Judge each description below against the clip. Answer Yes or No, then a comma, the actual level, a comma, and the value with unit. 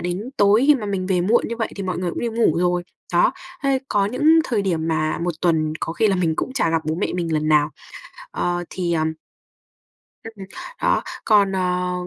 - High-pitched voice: No, medium, 180 Hz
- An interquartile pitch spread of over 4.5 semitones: No, average, 4.1 semitones